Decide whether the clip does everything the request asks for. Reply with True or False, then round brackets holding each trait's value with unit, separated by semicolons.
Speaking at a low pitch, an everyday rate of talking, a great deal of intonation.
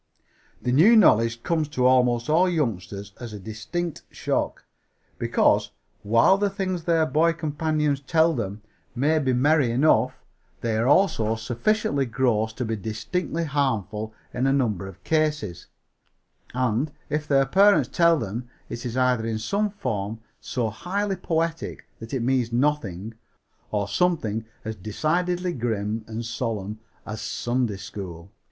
True (125 Hz; 145 wpm; 6.2 semitones)